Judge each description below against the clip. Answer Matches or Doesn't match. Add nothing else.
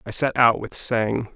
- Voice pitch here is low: Matches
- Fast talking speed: Matches